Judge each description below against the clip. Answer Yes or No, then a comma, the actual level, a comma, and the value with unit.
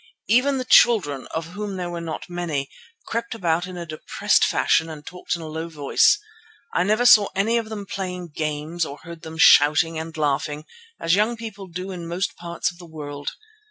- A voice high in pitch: No, medium, 170 Hz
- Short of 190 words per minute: No, average, 195 wpm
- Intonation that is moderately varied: Yes, average, 3.9 semitones